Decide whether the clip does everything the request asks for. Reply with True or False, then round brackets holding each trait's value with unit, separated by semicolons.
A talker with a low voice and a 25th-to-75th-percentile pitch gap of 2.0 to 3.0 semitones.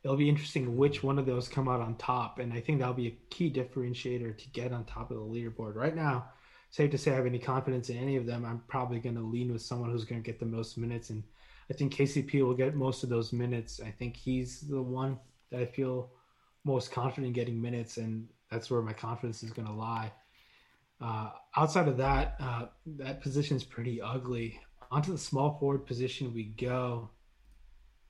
True (125 Hz; 2.5 semitones)